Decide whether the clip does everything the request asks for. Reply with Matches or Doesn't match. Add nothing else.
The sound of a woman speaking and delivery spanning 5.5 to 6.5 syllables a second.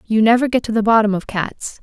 Matches